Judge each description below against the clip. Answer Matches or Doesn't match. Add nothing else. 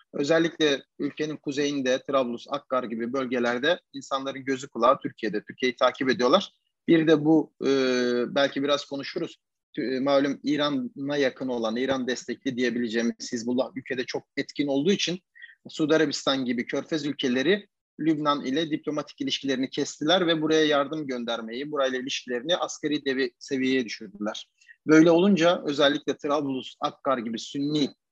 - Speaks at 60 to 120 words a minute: Doesn't match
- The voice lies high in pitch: Doesn't match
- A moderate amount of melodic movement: Matches